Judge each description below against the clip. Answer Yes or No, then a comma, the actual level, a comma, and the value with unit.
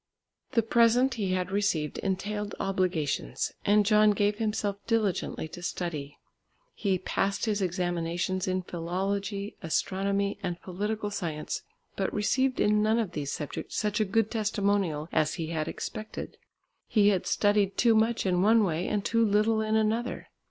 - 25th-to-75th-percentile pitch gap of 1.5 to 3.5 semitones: Yes, average, 3.0 semitones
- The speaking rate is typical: Yes, average, 150 wpm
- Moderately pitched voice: No, high, 200 Hz